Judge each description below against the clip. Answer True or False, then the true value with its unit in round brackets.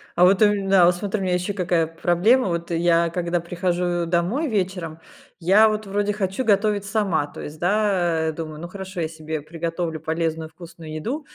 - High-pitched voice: False (175 Hz)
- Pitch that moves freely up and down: False (3.2 semitones)